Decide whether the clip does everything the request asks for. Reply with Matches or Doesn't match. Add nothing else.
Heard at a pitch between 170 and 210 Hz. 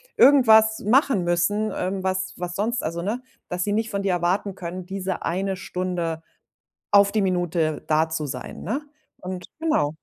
Matches